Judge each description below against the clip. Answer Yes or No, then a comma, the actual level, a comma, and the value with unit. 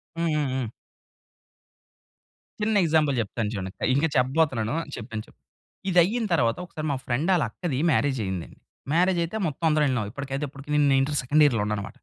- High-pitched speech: No, medium, 140 Hz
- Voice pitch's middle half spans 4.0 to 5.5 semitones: Yes, average, 4.9 semitones